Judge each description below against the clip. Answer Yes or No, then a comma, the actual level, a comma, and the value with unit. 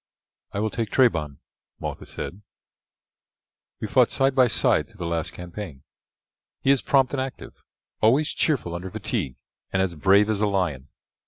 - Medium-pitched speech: No, low, 100 Hz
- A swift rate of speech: No, average, 160 wpm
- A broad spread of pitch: Yes, wide, 7.0 semitones